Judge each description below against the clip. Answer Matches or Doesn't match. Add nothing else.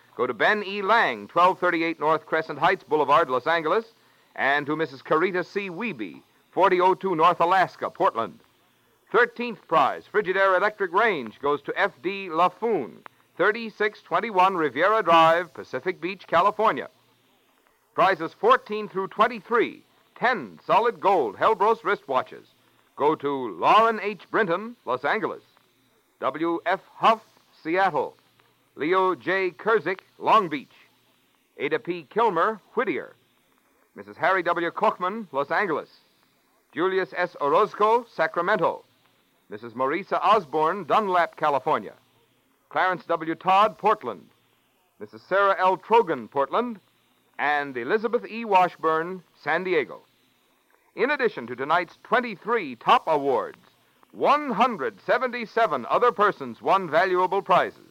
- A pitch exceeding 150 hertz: Matches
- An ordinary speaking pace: Doesn't match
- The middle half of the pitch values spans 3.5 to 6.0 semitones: Matches